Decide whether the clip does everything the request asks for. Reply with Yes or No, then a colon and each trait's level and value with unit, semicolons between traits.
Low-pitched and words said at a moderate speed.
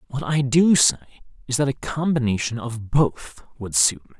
Yes: low, 125 Hz; average, 185 wpm